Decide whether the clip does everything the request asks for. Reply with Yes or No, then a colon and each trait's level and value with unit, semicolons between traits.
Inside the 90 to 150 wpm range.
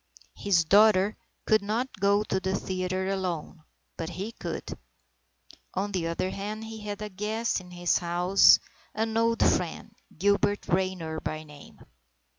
Yes: average, 145 wpm